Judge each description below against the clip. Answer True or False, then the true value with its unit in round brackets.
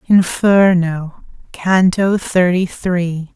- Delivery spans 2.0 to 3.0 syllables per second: True (2.8 syllables/s)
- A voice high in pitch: False (180 Hz)